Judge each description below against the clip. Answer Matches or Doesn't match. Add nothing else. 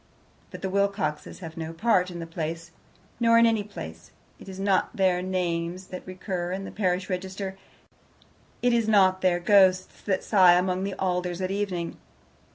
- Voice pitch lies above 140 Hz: Matches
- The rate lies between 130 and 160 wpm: Doesn't match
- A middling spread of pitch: Doesn't match